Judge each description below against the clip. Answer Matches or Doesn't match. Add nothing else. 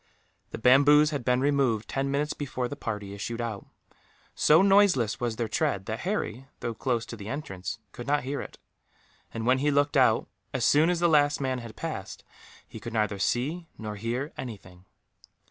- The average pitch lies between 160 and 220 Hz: Doesn't match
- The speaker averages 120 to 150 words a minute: Doesn't match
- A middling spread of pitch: Matches